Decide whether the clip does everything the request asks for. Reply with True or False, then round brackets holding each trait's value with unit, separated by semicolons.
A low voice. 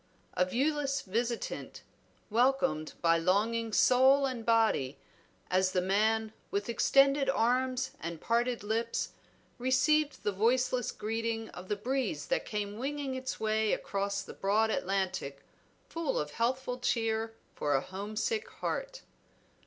False (225 Hz)